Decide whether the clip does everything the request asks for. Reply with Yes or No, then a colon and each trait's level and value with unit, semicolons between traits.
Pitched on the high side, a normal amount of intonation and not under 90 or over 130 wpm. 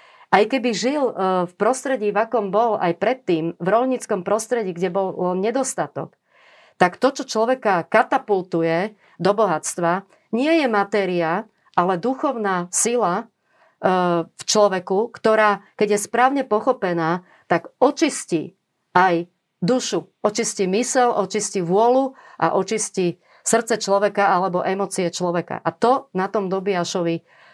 Yes: high, 205 Hz; average, 4.4 semitones; average, 120 wpm